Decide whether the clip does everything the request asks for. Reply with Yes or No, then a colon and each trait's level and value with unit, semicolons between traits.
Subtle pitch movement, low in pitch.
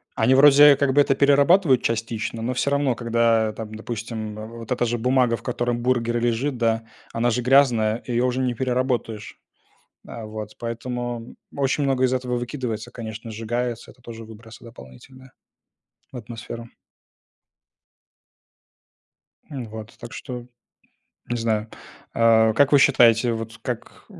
Yes: narrow, 2.2 semitones; low, 120 Hz